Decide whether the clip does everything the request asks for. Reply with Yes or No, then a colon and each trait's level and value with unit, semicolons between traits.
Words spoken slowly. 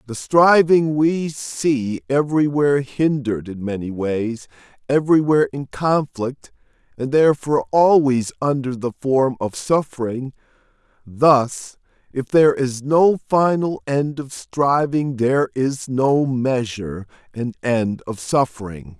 Yes: slow, 115 wpm